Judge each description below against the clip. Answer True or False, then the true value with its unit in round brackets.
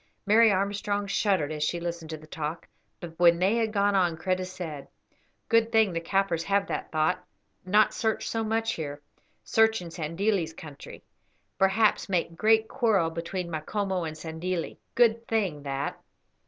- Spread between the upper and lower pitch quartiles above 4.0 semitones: True (4.6 semitones)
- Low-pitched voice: False (185 Hz)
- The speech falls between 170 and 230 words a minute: False (160 wpm)